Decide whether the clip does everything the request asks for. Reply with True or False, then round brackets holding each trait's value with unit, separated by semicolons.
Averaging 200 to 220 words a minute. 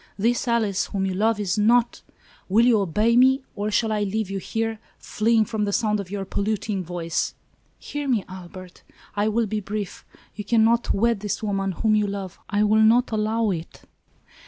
True (205 wpm)